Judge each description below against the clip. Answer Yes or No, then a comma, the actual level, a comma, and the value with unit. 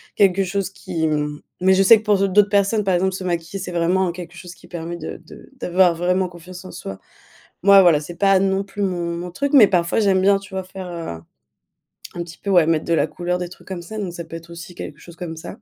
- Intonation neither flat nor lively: No, narrow, 2.2 semitones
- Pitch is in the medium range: Yes, medium, 180 Hz